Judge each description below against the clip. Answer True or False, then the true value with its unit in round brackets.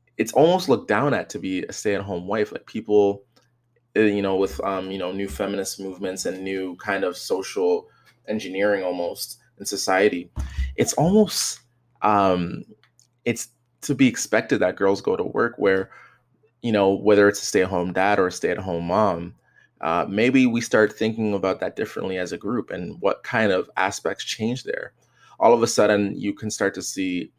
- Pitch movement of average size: True (3.9 semitones)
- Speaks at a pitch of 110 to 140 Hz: False (100 Hz)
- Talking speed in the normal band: True (180 wpm)